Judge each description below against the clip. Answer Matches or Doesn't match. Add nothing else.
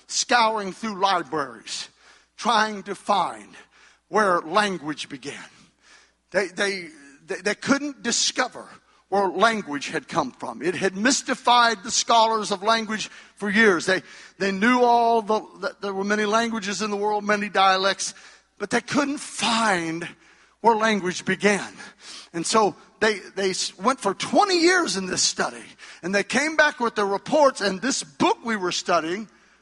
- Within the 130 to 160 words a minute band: Matches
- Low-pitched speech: Doesn't match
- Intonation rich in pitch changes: Doesn't match